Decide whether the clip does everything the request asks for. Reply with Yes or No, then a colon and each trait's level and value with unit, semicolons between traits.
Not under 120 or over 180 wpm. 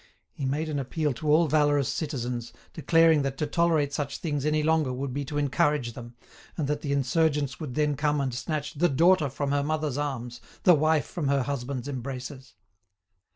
No: average, 190 wpm